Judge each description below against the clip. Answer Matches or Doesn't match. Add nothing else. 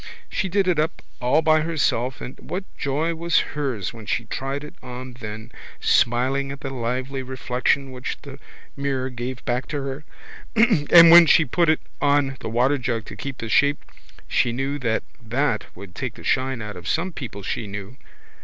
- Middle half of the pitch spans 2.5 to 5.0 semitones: Matches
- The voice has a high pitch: Doesn't match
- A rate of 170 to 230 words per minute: Matches